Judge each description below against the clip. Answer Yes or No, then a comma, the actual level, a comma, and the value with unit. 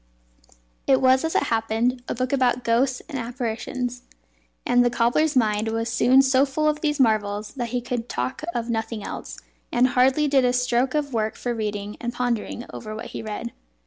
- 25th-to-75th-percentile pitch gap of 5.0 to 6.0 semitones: No, narrow, 2.5 semitones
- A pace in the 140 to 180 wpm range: No, average, 190 wpm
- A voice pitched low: No, high, 245 Hz